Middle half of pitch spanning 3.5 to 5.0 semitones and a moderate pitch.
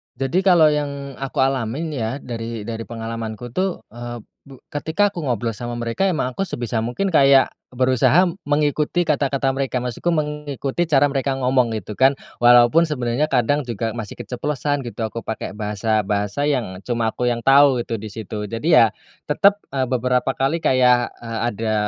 No: average, 3.9 semitones; low, 125 Hz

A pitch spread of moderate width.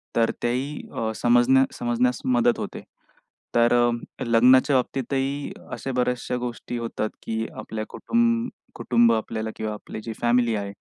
No: narrow, 2.2 semitones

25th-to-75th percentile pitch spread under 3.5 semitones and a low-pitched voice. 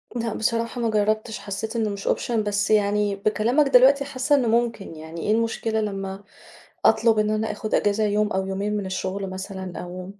No: narrow, 2.6 semitones; high, 210 Hz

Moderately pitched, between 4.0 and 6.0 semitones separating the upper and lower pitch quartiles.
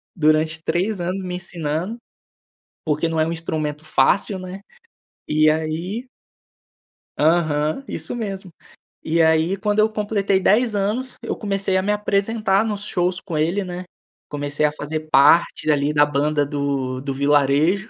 Yes: medium, 170 Hz; average, 4.6 semitones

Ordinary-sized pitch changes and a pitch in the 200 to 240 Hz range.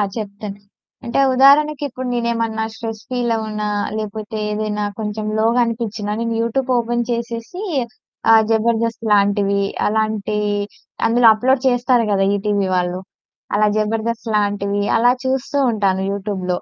No: narrow, 2.2 semitones; high, 220 Hz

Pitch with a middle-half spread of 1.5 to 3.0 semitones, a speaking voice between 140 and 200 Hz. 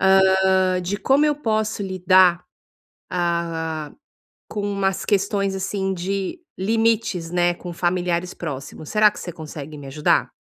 Yes: narrow, 2.6 semitones; medium, 185 Hz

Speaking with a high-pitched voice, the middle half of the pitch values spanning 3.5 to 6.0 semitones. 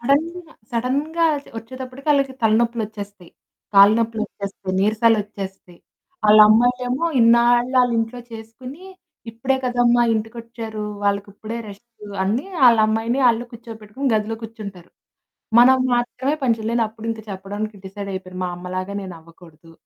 No: high, 225 Hz; average, 3.1 semitones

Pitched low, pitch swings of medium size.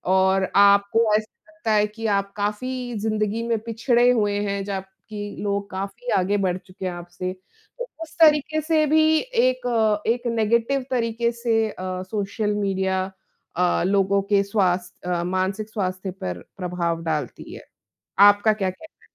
No: high, 205 Hz; average, 3.5 semitones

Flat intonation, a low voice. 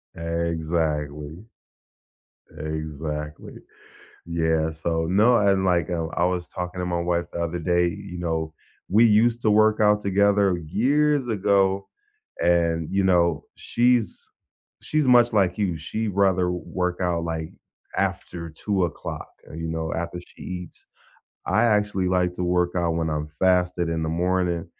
No: average, 3.3 semitones; very low, 90 Hz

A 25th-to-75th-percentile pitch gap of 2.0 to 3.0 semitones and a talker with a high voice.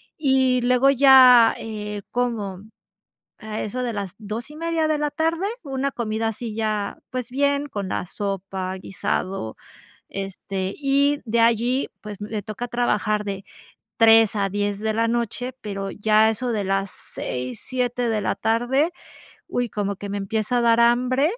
No: average, 3.7 semitones; high, 225 Hz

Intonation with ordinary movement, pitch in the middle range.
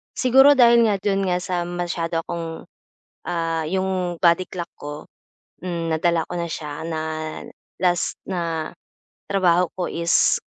No: narrow, 2.0 semitones; medium, 175 Hz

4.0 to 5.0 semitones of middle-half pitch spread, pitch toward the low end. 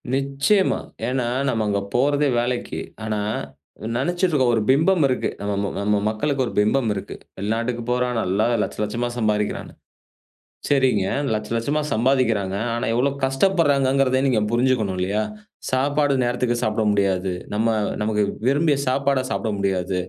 Yes: average, 4.4 semitones; low, 120 Hz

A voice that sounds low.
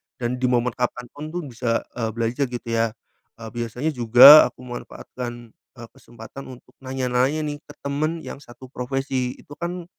Yes: low, 125 Hz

